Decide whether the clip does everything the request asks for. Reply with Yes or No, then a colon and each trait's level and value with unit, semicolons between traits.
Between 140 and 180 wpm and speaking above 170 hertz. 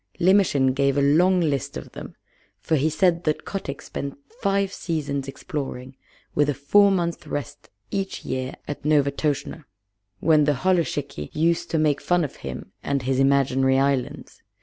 No: average, 155 wpm; medium, 145 Hz